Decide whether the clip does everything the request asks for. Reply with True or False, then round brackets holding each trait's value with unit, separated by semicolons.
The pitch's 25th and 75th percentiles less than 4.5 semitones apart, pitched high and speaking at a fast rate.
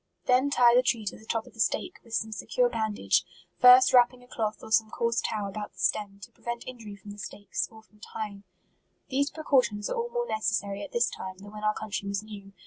True (3.3 semitones; 220 Hz; 230 wpm)